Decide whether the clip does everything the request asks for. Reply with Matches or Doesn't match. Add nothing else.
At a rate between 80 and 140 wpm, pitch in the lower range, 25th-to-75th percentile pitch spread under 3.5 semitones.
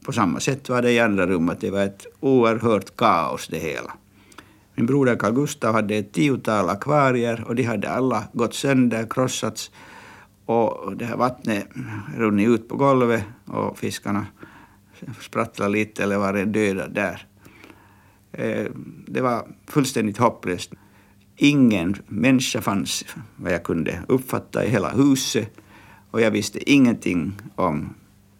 Doesn't match